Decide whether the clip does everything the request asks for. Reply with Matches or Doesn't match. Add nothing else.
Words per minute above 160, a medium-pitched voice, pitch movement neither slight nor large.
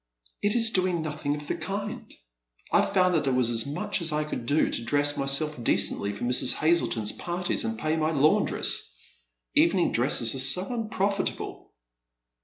Doesn't match